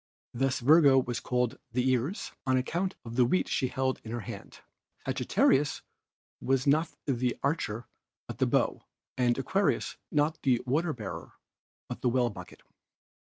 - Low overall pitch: Yes, low, 130 Hz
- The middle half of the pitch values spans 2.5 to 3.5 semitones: Yes, average, 3.1 semitones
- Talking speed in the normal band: Yes, average, 155 wpm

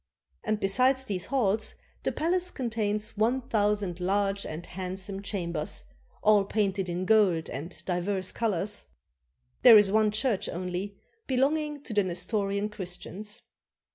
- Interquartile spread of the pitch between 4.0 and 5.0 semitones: No, average, 2.8 semitones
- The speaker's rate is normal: No, slow, 130 wpm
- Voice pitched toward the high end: Yes, high, 205 Hz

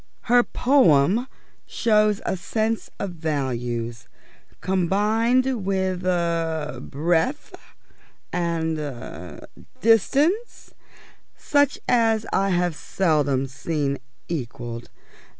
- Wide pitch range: Yes, wide, 7.3 semitones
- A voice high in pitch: No, medium, 175 Hz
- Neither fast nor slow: No, slow, 80 wpm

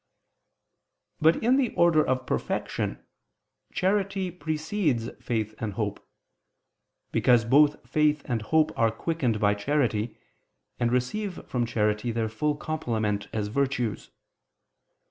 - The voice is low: Yes, low, 125 Hz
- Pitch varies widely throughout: Yes, wide, 6.0 semitones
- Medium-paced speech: No, slow, 115 wpm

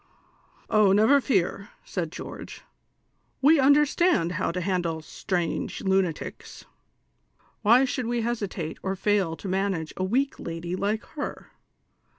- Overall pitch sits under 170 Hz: No, high, 195 Hz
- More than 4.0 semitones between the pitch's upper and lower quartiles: Yes, average, 5.3 semitones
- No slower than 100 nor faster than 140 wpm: Yes, slow, 135 wpm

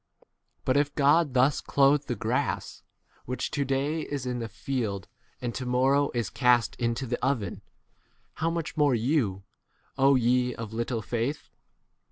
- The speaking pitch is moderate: No, low, 125 Hz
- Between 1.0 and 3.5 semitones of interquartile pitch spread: Yes, average, 3.1 semitones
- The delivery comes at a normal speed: Yes, average, 160 wpm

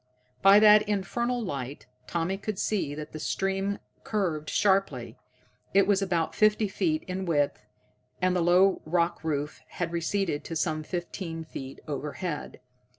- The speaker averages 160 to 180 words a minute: No, average, 145 wpm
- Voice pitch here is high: No, medium, 180 Hz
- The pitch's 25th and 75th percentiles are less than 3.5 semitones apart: No, average, 4.0 semitones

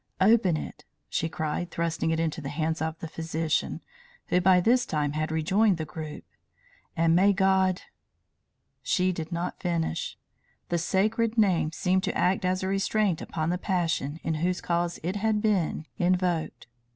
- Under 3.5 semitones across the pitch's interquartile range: Yes, average, 2.8 semitones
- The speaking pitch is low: No, medium, 175 Hz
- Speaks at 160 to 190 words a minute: Yes, average, 165 wpm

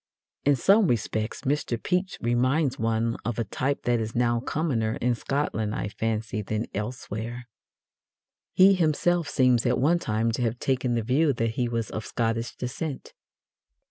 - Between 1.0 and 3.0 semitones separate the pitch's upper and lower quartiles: No, average, 3.6 semitones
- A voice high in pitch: No, low, 120 Hz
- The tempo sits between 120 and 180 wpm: Yes, average, 160 wpm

